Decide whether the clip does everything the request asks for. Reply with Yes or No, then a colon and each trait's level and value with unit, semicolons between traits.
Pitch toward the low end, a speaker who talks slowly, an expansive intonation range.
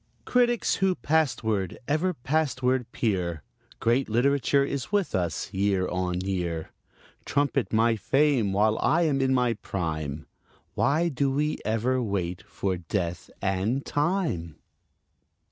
Yes: low, 115 Hz; slow, 125 wpm; wide, 7.2 semitones